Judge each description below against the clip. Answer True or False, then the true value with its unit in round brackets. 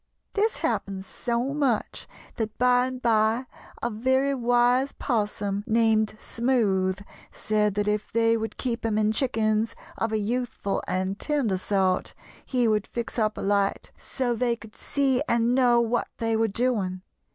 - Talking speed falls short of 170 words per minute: True (155 wpm)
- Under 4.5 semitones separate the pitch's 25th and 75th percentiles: True (2.8 semitones)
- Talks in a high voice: True (225 Hz)